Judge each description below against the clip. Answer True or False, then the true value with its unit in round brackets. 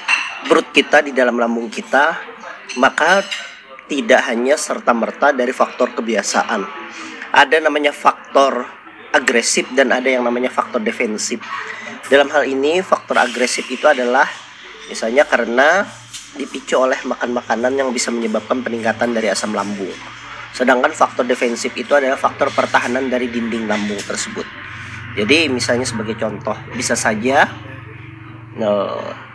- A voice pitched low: True (120 Hz)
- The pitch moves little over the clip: True (2.3 semitones)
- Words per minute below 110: False (125 wpm)